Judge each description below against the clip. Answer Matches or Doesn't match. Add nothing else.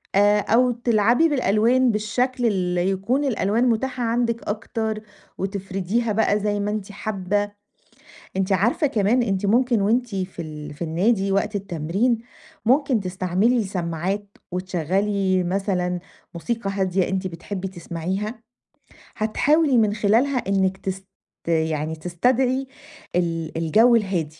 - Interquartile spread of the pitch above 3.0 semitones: Matches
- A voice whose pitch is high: Matches